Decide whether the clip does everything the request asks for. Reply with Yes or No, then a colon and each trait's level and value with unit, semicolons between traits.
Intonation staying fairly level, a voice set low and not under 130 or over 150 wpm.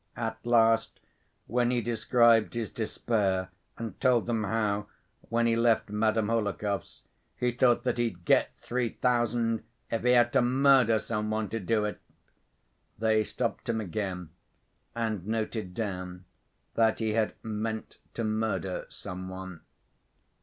Yes: narrow, 2.0 semitones; low, 110 Hz; average, 140 wpm